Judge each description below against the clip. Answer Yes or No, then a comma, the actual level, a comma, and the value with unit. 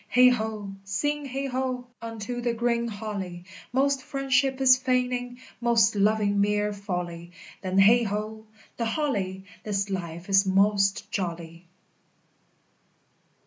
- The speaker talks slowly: Yes, slow, 120 wpm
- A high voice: Yes, high, 215 Hz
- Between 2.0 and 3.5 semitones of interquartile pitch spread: No, average, 4.2 semitones